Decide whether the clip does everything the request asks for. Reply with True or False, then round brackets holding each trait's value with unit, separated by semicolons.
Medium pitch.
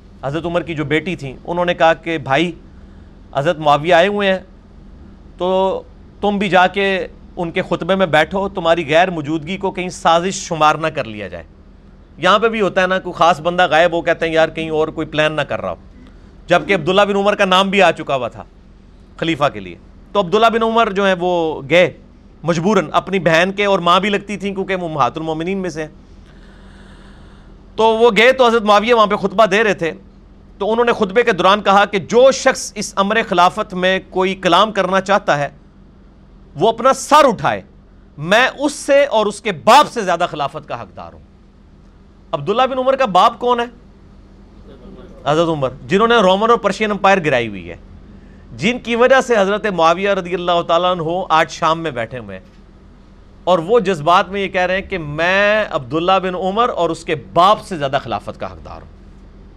True (175 Hz)